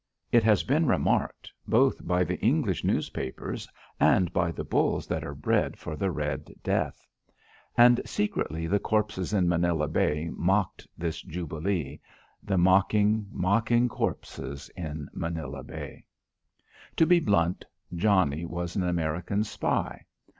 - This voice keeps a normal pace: No, slow, 130 wpm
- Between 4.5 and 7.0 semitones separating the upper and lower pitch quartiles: No, average, 4.1 semitones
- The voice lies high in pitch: No, very low, 90 Hz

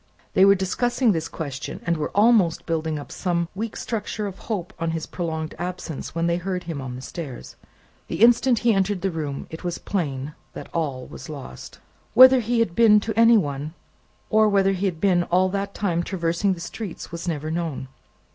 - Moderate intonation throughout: Yes, average, 4.1 semitones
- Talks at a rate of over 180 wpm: Yes, average, 200 wpm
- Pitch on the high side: No, medium, 175 Hz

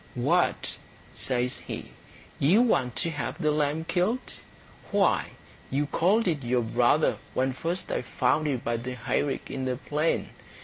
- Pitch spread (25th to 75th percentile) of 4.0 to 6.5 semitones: Yes, average, 4.5 semitones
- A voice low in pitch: No, medium, 145 Hz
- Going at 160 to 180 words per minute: No, average, 150 wpm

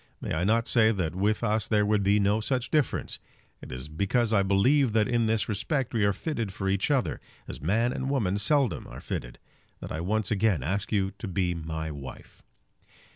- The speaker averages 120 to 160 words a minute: No, fast, 205 wpm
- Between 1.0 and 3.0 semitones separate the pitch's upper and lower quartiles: No, average, 3.5 semitones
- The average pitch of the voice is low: Yes, low, 105 Hz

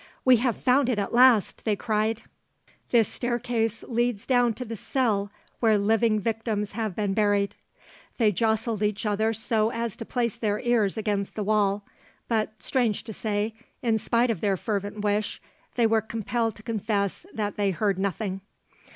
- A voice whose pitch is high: Yes, high, 220 Hz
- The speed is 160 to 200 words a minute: Yes, average, 170 wpm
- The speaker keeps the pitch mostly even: Yes, narrow, 2.1 semitones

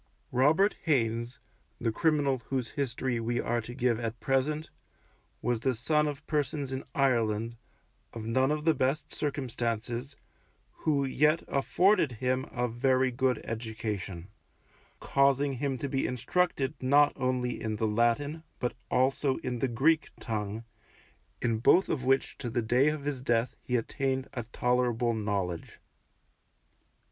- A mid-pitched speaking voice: No, low, 130 Hz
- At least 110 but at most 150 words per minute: Yes, average, 140 wpm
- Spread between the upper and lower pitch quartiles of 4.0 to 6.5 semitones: No, average, 3.2 semitones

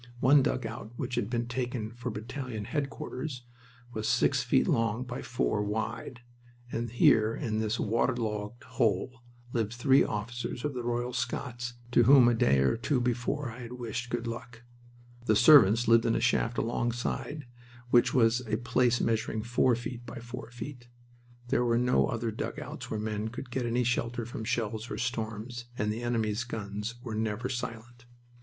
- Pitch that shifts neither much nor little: No, narrow, 1.8 semitones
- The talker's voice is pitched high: No, low, 120 Hz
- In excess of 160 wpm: Yes, average, 170 wpm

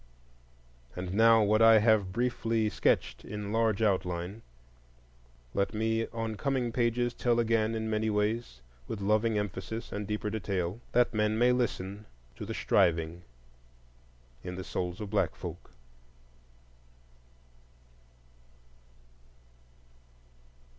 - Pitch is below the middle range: Yes, low, 110 Hz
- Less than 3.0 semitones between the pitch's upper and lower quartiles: Yes, narrow, 2.5 semitones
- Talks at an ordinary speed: No, slow, 115 wpm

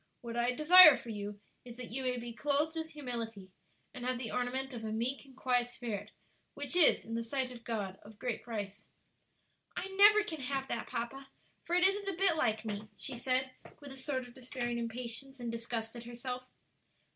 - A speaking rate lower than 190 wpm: No, fast, 205 wpm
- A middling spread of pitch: Yes, average, 3.0 semitones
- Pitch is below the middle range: No, high, 245 Hz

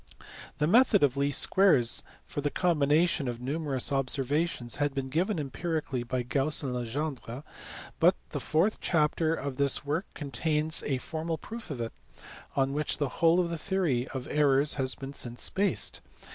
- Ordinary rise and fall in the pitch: Yes, average, 3.6 semitones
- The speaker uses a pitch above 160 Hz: No, medium, 145 Hz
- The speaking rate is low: No, average, 165 wpm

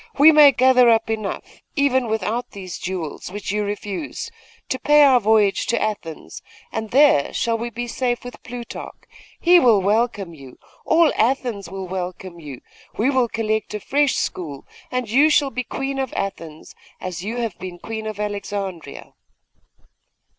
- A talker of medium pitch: No, high, 220 Hz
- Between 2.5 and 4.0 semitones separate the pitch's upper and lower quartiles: No, average, 4.7 semitones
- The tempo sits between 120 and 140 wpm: No, average, 160 wpm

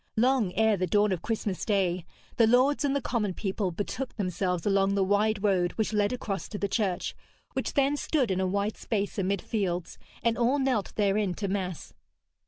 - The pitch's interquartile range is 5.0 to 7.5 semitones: No, average, 3.2 semitones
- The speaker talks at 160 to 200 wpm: Yes, average, 190 wpm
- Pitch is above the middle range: Yes, high, 205 Hz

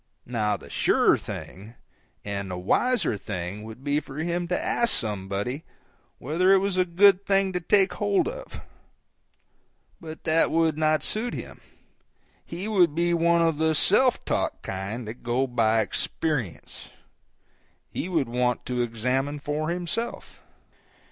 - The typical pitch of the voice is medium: Yes, medium, 155 Hz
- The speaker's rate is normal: Yes, average, 145 wpm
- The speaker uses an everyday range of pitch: No, wide, 7.5 semitones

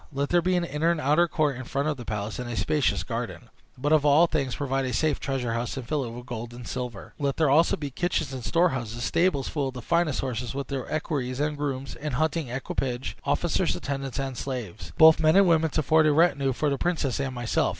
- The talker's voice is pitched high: No, medium, 140 Hz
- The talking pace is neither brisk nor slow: No, fast, 240 wpm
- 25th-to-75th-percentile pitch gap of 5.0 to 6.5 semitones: No, average, 3.7 semitones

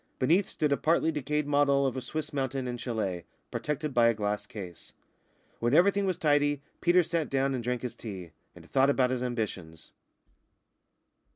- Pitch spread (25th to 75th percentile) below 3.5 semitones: No, average, 4.2 semitones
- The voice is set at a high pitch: No, low, 135 Hz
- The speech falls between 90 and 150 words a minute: No, average, 175 wpm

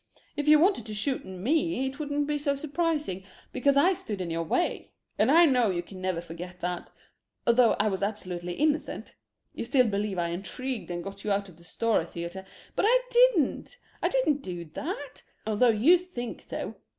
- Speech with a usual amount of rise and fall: No, wide, 7.9 semitones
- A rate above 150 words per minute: Yes, average, 190 wpm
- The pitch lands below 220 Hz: No, high, 230 Hz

